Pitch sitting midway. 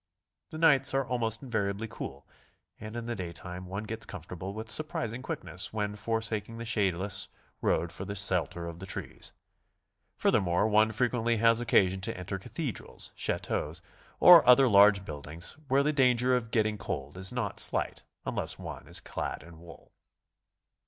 No: low, 105 Hz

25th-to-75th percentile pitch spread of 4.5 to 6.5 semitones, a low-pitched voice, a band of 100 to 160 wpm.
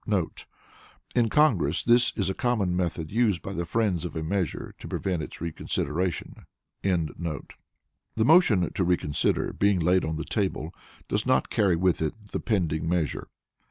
No: average, 3.8 semitones; very low, 90 Hz; average, 155 wpm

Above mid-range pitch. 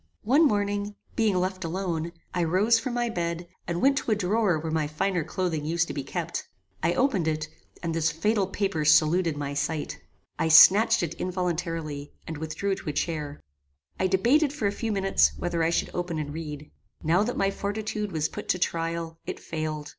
No: medium, 175 Hz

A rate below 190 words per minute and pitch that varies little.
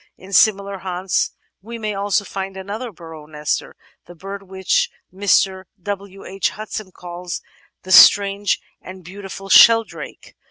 Yes: slow, 135 wpm; narrow, 1.5 semitones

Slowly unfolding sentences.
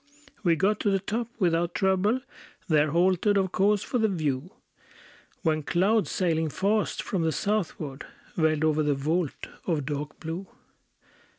No: average, 150 wpm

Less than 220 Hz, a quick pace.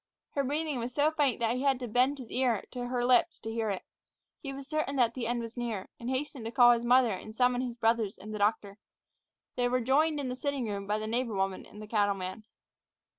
No: high, 245 Hz; fast, 240 wpm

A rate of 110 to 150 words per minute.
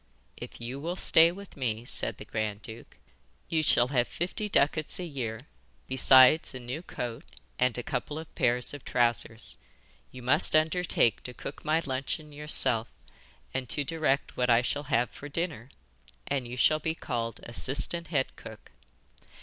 No: average, 165 wpm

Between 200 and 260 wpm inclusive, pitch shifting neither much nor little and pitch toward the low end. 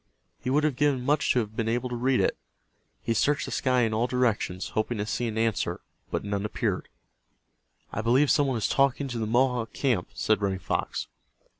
Yes: fast, 205 wpm; average, 3.4 semitones; low, 120 Hz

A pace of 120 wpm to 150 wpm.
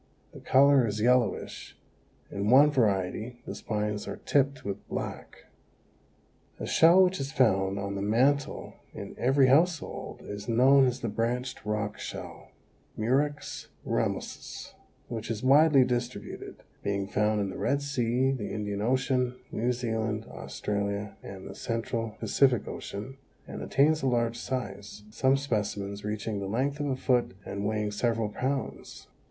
Yes: average, 145 wpm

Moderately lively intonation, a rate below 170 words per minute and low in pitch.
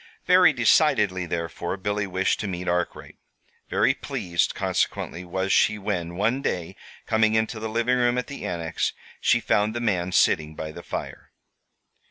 Yes: average, 4.2 semitones; average, 160 wpm; low, 100 Hz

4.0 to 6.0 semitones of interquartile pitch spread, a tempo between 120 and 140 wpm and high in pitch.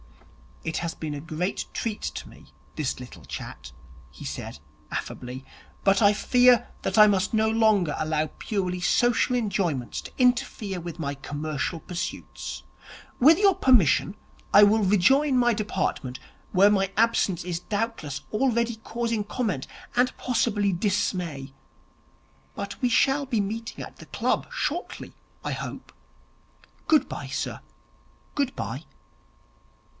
Yes: wide, 5.6 semitones; slow, 135 wpm; high, 205 Hz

